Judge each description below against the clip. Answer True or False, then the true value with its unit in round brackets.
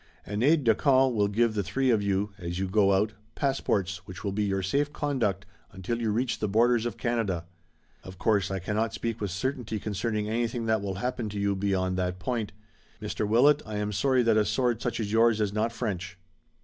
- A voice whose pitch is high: False (105 Hz)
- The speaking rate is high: True (215 wpm)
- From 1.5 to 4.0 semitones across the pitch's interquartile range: True (3.2 semitones)